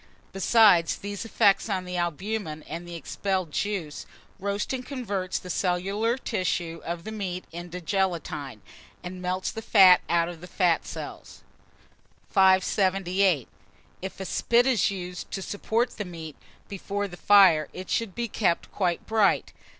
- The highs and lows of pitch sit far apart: No, average, 2.7 semitones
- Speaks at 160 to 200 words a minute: No, average, 145 wpm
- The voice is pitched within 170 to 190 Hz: Yes, medium, 185 Hz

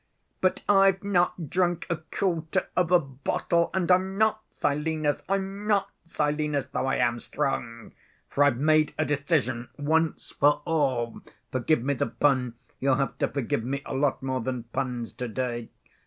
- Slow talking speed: No, average, 160 wpm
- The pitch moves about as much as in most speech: Yes, average, 4.9 semitones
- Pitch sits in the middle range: Yes, medium, 145 Hz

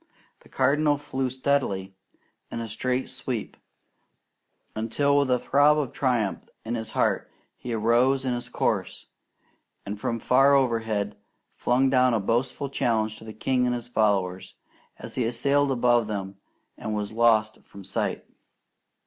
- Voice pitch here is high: No, low, 120 Hz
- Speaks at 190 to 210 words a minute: No, average, 150 wpm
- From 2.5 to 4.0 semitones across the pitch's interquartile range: Yes, average, 3.4 semitones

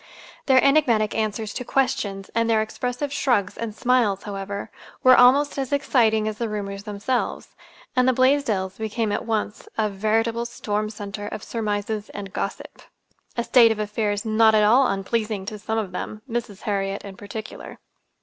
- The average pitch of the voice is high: Yes, high, 220 Hz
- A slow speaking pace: No, average, 160 wpm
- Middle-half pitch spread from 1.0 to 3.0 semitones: Yes, narrow, 2.6 semitones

